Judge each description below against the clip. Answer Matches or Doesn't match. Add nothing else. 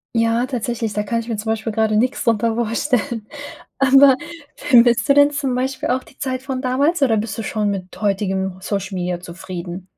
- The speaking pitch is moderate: Doesn't match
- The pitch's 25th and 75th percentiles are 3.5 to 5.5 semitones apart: Matches